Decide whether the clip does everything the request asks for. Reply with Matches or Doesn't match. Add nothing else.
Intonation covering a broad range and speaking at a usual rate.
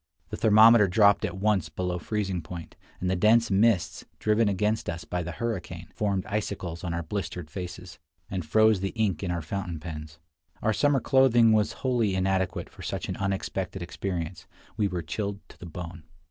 Doesn't match